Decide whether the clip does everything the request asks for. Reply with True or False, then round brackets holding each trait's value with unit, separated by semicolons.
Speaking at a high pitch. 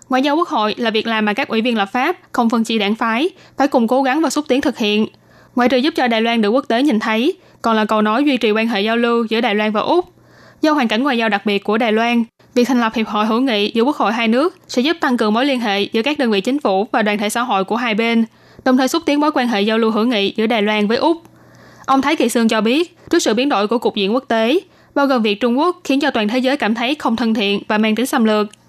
True (235 Hz)